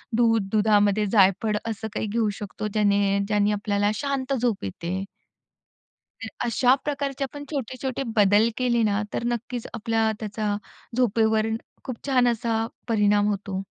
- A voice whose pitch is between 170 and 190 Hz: No, high, 220 Hz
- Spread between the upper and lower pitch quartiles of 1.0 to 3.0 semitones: Yes, average, 2.7 semitones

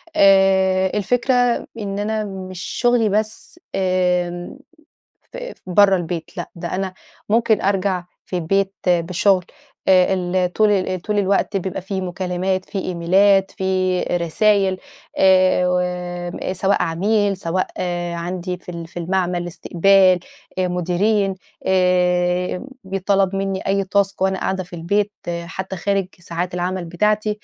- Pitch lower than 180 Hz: No, medium, 185 Hz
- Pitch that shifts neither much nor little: No, narrow, 1.7 semitones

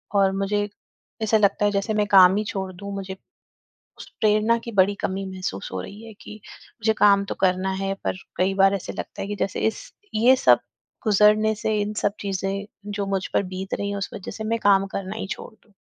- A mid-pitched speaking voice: No, high, 200 Hz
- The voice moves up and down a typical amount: No, narrow, 1.6 semitones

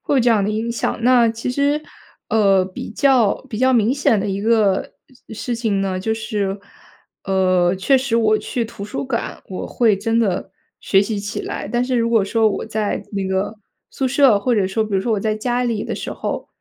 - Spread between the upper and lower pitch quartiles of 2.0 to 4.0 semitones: Yes, average, 3.3 semitones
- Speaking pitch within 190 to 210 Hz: No, high, 220 Hz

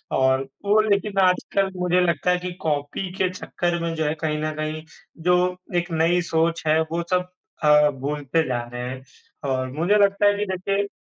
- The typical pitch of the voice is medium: Yes, medium, 170 Hz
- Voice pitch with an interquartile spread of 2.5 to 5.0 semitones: Yes, average, 3.3 semitones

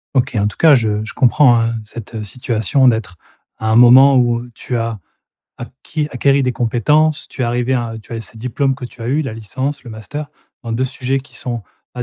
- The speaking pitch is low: Yes, low, 120 Hz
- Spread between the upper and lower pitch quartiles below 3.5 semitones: Yes, average, 2.8 semitones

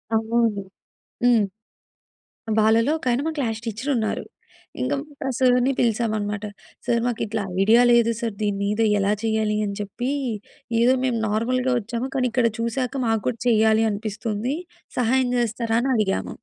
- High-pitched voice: Yes, high, 230 Hz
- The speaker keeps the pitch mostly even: Yes, narrow, 2.3 semitones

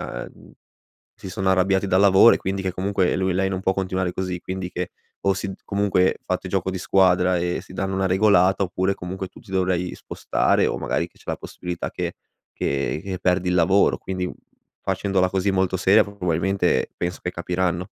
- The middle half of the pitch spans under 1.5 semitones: Yes, narrow, 1.1 semitones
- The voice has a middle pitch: No, very low, 95 Hz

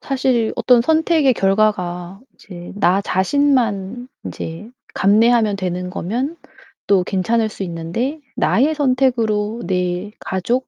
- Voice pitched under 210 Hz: No, high, 215 Hz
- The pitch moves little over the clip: No, average, 5.2 semitones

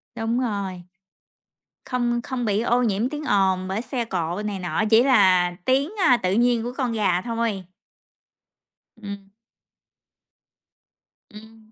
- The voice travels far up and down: No, average, 3.9 semitones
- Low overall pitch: No, high, 220 Hz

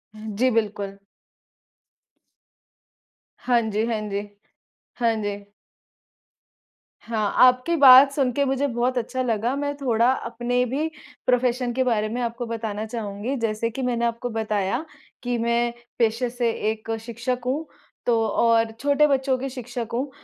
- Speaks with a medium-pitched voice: No, high, 240 Hz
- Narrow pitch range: Yes, narrow, 2.3 semitones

